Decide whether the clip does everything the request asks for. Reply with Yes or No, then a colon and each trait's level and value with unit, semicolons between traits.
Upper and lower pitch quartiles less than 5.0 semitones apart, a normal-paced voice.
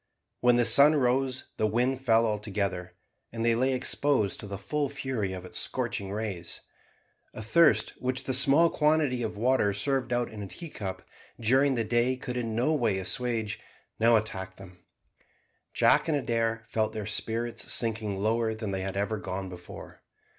Yes: average, 3.9 semitones; average, 170 wpm